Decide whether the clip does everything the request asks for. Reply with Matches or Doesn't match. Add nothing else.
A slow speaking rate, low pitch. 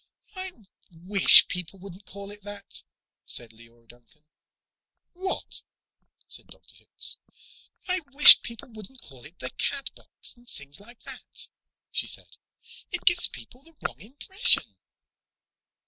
Doesn't match